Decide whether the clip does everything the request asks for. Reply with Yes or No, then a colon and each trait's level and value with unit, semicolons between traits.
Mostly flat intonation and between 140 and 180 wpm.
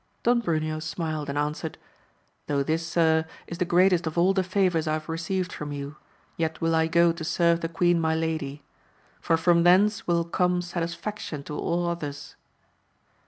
Yes: narrow, 1.8 semitones; average, 175 wpm